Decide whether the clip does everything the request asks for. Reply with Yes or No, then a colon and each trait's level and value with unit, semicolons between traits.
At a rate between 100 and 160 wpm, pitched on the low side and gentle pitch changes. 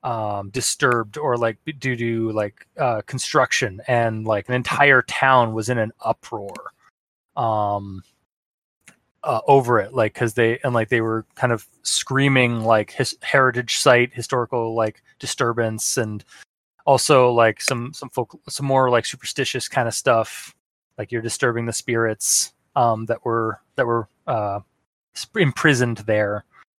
Yes: average, 150 wpm; low, 115 Hz; narrow, 2.2 semitones